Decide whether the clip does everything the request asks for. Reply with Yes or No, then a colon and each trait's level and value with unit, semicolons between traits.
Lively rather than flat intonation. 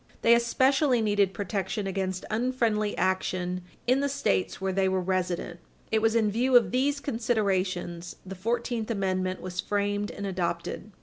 No: average, 3.9 semitones